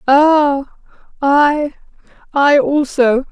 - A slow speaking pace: Yes, slow, 55 wpm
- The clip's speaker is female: Yes, female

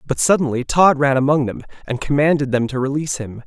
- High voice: No, medium, 140 Hz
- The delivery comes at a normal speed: No, fast, 210 wpm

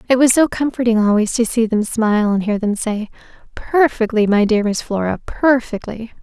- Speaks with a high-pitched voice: Yes, high, 225 Hz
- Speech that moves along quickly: No, average, 185 wpm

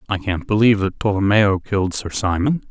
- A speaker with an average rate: Yes, average, 175 wpm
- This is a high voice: No, low, 100 Hz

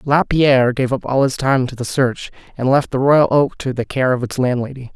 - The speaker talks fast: Yes, fast, 240 wpm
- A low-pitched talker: Yes, low, 130 Hz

